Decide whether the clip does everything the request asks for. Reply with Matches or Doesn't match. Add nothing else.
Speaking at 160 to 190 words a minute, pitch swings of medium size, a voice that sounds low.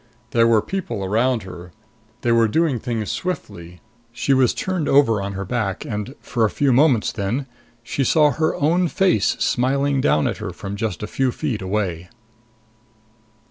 Doesn't match